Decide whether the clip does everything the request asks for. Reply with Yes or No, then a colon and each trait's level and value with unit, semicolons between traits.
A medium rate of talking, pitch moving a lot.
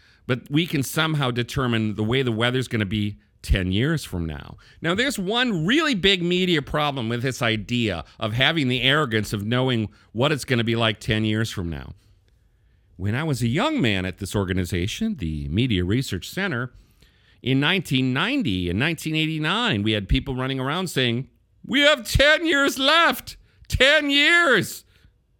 Yes: average, 165 wpm; wide, 6.9 semitones